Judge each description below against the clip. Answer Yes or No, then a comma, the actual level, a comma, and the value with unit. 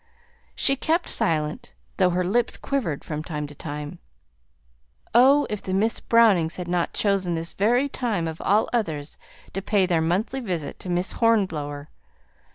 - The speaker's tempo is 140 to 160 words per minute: Yes, average, 155 wpm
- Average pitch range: No, wide, 6.0 semitones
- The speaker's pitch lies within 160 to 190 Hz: Yes, medium, 185 Hz